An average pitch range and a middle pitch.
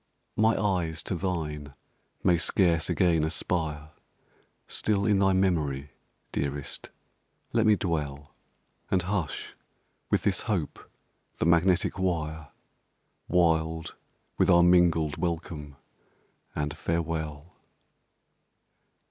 No: average, 3.1 semitones; very low, 85 Hz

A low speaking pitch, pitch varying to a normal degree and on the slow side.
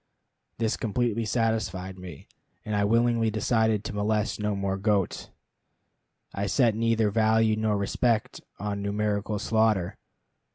No: low, 105 Hz; narrow, 1.8 semitones; slow, 125 wpm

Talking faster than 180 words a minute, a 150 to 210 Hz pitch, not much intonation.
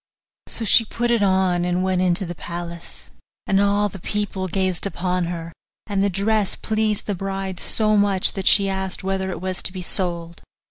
Yes: average, 190 wpm; high, 190 Hz; narrow, 2.1 semitones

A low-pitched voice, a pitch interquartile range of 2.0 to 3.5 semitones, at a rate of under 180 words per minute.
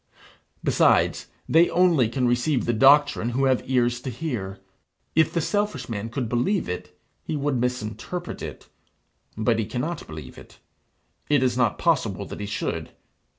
No: low, 125 Hz; average, 4.6 semitones; average, 155 wpm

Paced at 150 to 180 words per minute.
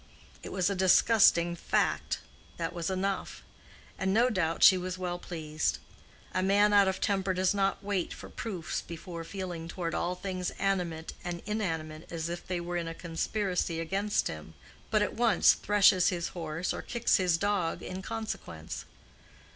Yes: average, 165 wpm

